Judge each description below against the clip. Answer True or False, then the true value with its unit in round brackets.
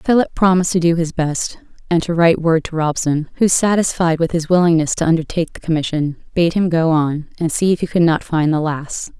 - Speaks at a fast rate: True (220 wpm)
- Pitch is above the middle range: False (165 Hz)